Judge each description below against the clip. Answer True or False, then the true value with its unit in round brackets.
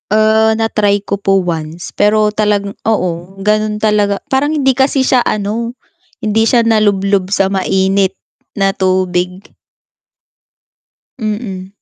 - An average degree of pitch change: False (2.1 semitones)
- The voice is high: True (205 Hz)